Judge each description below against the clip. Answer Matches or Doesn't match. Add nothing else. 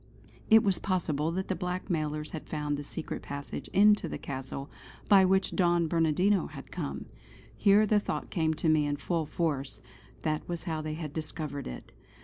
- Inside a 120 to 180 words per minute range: Matches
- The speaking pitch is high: Doesn't match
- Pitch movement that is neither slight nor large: Matches